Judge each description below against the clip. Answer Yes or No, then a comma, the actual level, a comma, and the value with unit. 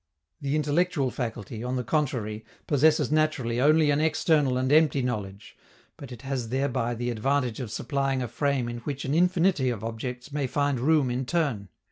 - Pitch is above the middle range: No, low, 135 Hz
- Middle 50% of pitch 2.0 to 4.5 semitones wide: Yes, average, 3.5 semitones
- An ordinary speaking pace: Yes, average, 175 wpm